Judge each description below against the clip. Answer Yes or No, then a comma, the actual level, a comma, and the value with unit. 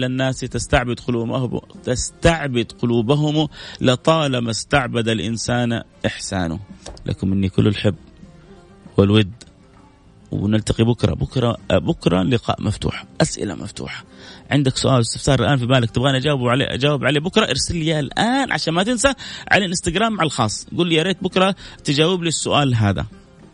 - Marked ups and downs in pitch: Yes, wide, 6.5 semitones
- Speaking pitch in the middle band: No, low, 130 Hz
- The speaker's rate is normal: No, fast, 140 wpm